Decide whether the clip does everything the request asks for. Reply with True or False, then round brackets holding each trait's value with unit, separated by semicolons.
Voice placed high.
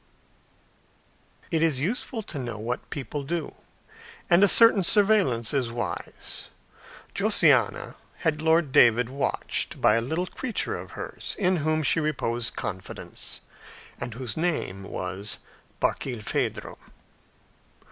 False (145 Hz)